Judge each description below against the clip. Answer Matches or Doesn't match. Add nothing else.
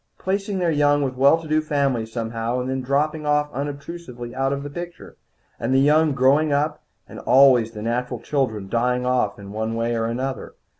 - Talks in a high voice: Doesn't match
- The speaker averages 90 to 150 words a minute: Doesn't match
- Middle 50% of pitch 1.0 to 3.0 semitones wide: Doesn't match